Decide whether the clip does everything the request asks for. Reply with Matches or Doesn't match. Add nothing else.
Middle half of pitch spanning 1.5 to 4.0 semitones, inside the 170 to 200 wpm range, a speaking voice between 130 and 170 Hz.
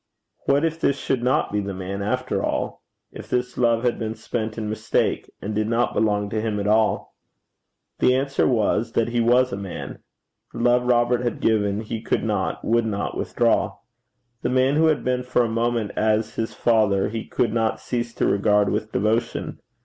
Doesn't match